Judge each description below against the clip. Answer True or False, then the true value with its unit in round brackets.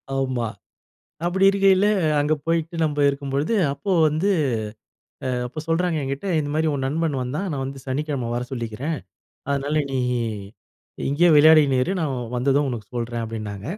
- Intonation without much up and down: False (3.5 semitones)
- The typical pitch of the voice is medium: True (145 Hz)